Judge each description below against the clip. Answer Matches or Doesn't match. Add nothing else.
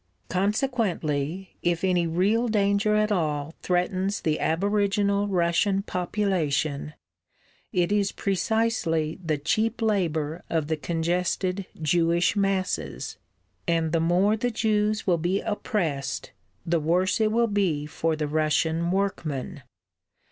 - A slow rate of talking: Matches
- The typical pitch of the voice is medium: Matches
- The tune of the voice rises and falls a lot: Doesn't match